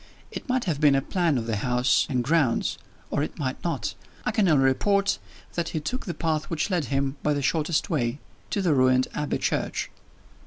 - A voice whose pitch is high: No, medium, 150 Hz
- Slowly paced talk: No, fast, 205 wpm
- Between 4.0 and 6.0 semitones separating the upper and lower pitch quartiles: Yes, average, 4.4 semitones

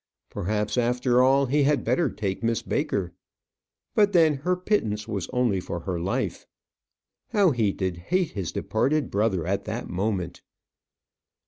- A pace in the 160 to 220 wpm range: No, average, 145 wpm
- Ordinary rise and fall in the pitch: No, wide, 6.4 semitones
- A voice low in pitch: Yes, low, 110 Hz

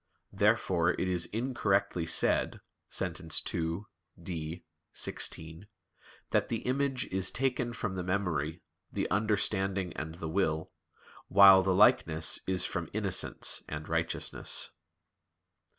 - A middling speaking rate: No, slow, 115 wpm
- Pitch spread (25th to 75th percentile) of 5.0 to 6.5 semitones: No, average, 3.5 semitones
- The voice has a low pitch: Yes, very low, 95 Hz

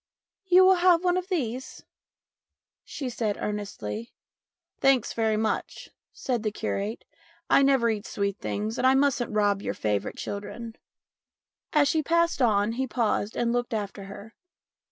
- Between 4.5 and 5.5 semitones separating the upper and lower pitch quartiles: Yes, average, 4.8 semitones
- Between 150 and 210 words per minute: Yes, average, 155 wpm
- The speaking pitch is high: Yes, high, 235 Hz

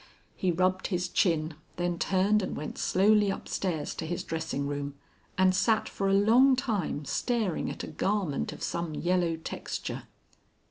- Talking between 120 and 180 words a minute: Yes, average, 155 wpm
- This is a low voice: No, medium, 185 Hz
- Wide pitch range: No, average, 3.8 semitones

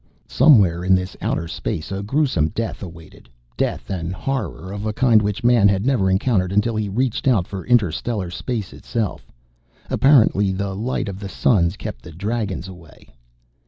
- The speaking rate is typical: Yes, average, 170 wpm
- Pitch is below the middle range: Yes, low, 100 Hz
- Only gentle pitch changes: No, average, 3.9 semitones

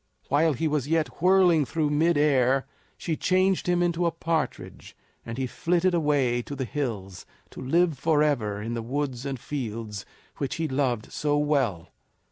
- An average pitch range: Yes, average, 4.9 semitones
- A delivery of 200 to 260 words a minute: No, average, 165 wpm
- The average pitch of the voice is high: No, medium, 145 Hz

